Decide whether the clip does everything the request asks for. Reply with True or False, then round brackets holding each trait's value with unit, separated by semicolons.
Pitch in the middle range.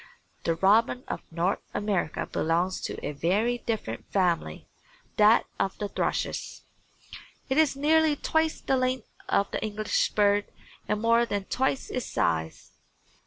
False (210 Hz)